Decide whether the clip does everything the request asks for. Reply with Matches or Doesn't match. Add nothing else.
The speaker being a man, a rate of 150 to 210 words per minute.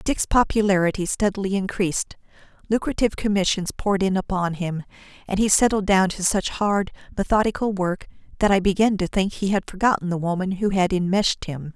Doesn't match